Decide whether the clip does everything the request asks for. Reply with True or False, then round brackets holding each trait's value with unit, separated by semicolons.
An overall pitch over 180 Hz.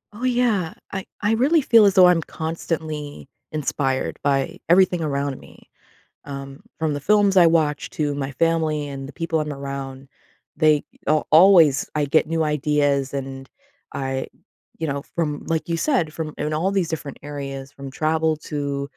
False (150 Hz)